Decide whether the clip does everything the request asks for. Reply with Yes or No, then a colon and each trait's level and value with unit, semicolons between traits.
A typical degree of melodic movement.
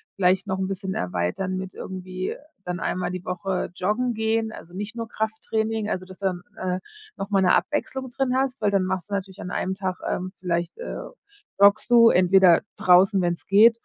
Yes: average, 3.1 semitones